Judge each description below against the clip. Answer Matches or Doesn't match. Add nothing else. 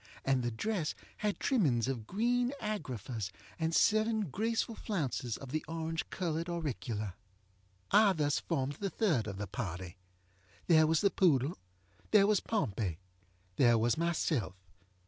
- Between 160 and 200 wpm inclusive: Doesn't match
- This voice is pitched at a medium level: Matches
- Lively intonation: Matches